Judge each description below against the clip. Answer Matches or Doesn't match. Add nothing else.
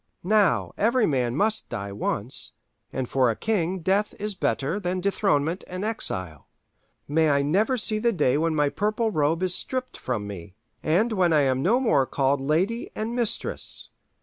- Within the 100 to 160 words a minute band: Doesn't match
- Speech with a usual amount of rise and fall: Doesn't match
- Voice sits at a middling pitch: Matches